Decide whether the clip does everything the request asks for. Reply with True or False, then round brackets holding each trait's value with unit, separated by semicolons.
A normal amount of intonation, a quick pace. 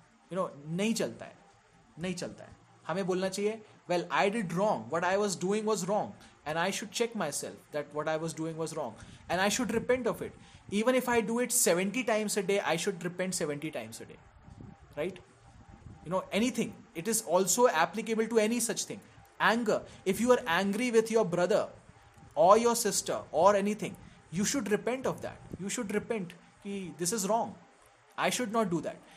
True (4.5 semitones; 205 wpm)